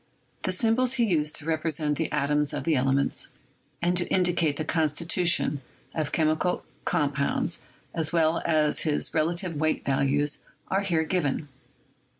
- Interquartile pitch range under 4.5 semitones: Yes, average, 2.7 semitones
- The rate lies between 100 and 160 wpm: Yes, average, 155 wpm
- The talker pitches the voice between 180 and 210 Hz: No, medium, 155 Hz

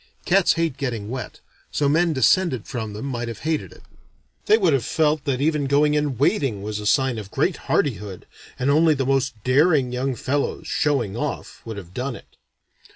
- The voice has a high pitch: No, low, 135 Hz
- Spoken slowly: No, average, 185 wpm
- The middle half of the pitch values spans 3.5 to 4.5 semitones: Yes, average, 4.1 semitones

